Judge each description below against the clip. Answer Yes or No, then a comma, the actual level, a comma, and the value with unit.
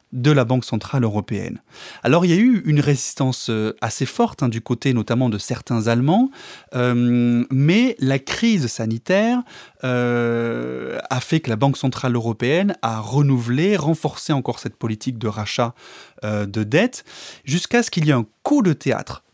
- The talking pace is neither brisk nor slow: Yes, average, 170 wpm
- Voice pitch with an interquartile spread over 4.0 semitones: Yes, average, 4.7 semitones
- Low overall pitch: Yes, low, 125 Hz